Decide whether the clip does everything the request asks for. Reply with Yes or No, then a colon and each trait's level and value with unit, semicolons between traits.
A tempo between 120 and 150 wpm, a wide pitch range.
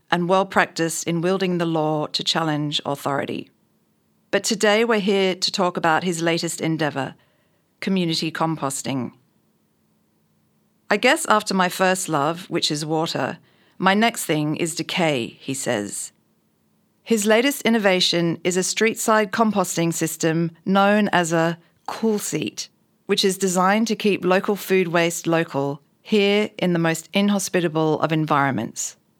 No: average, 140 wpm; average, 3.8 semitones